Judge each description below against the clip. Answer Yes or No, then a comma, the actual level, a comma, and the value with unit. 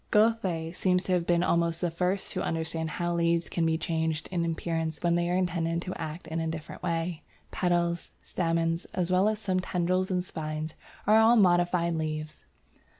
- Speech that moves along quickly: No, average, 185 wpm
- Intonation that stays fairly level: Yes, narrow, 1.9 semitones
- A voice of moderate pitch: Yes, medium, 170 Hz